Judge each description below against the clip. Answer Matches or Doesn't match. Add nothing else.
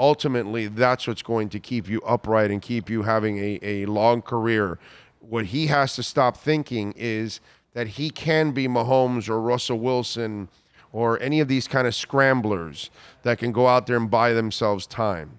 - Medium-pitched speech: Doesn't match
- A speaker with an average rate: Matches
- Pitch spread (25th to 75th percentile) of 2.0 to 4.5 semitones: Matches